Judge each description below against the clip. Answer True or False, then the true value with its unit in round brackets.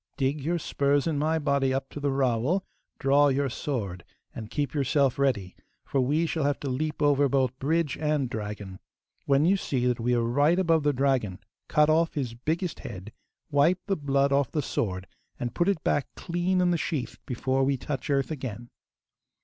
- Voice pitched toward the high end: False (140 Hz)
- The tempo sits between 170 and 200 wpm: True (190 wpm)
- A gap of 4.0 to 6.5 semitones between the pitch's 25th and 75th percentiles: False (3.3 semitones)